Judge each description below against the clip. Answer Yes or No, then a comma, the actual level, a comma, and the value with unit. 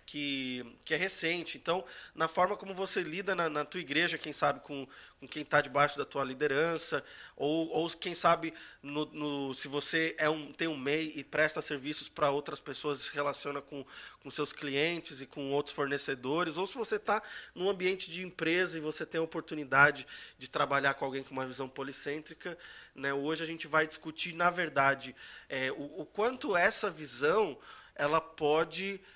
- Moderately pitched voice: Yes, medium, 155 Hz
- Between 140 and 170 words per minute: No, fast, 185 wpm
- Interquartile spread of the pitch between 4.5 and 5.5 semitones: No, average, 3.0 semitones